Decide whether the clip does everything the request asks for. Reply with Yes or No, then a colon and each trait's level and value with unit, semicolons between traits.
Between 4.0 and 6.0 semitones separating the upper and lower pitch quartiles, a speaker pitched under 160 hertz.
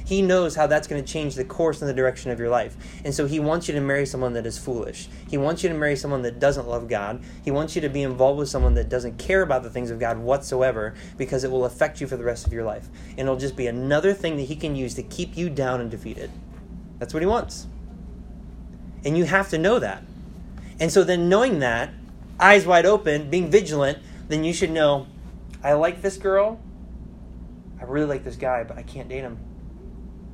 Yes: average, 4.8 semitones; medium, 140 Hz